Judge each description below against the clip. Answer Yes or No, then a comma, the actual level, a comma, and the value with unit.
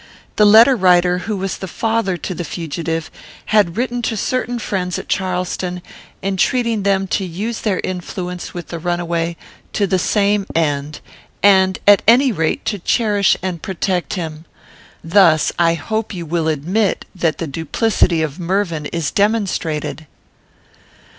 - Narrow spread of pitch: No, average, 3.6 semitones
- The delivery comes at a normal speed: Yes, average, 145 wpm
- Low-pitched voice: No, medium, 185 Hz